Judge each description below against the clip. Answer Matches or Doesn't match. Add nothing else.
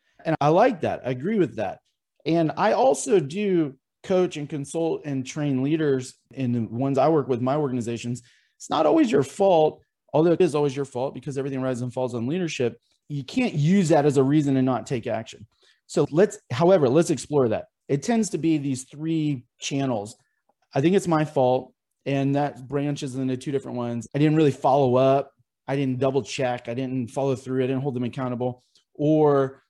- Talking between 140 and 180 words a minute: Doesn't match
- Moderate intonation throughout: Matches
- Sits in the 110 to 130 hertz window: Doesn't match